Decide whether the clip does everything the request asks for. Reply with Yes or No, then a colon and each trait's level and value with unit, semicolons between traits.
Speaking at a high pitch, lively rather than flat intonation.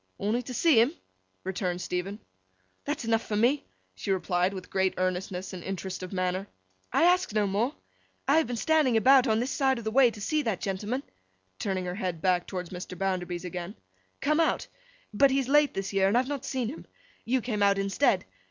Yes: high, 205 Hz; wide, 5.8 semitones